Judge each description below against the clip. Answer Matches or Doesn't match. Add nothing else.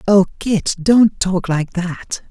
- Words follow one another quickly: Doesn't match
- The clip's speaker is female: Doesn't match